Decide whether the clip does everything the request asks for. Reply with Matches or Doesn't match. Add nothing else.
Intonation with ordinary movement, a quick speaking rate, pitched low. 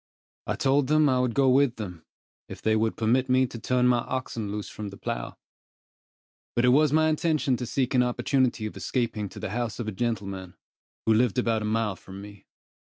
Matches